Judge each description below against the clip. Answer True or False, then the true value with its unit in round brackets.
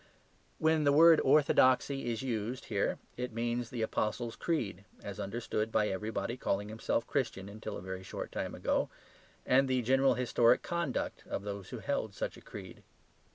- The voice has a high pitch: False (120 Hz)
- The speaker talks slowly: False (165 wpm)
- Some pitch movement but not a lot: True (3.8 semitones)